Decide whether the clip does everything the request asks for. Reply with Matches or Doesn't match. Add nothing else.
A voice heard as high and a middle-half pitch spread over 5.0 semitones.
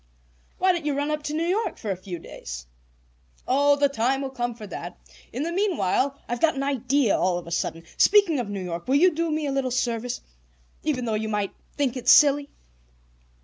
Matches